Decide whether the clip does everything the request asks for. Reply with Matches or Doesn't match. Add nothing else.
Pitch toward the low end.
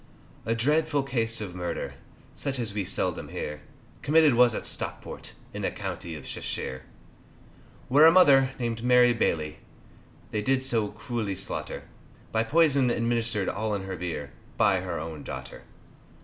Matches